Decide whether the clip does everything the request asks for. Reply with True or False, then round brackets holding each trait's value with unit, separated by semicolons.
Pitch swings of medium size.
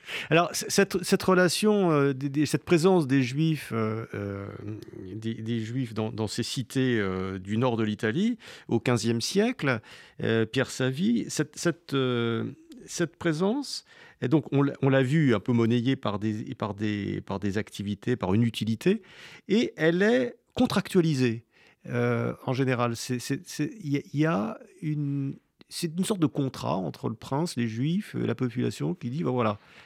False (6.4 semitones)